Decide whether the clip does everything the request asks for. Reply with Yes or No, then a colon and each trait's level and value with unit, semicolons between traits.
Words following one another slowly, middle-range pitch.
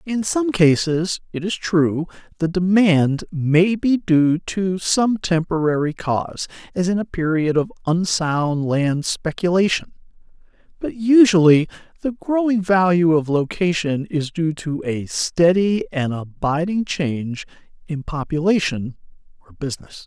Yes: slow, 125 wpm; medium, 170 Hz